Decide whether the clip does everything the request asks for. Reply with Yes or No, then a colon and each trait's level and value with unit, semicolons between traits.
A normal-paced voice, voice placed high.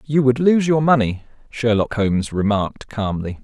No: average, 155 wpm; low, 120 Hz